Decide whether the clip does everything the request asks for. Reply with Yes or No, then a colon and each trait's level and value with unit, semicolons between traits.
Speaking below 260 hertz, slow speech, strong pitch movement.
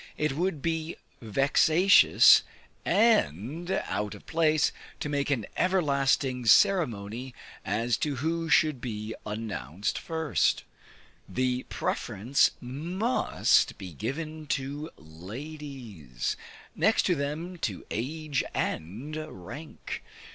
Yes: medium, 140 Hz; slow, 100 wpm; wide, 6.0 semitones